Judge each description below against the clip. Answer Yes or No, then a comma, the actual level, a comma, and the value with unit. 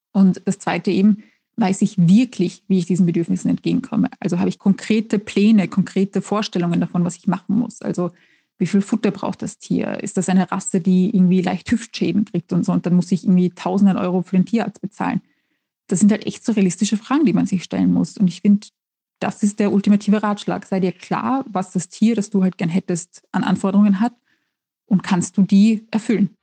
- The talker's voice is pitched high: Yes, high, 195 Hz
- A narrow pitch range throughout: Yes, narrow, 2.3 semitones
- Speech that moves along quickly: Yes, fast, 210 wpm